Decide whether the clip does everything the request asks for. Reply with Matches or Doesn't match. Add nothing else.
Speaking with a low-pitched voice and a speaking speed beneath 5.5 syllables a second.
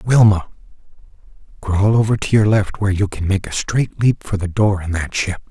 Matches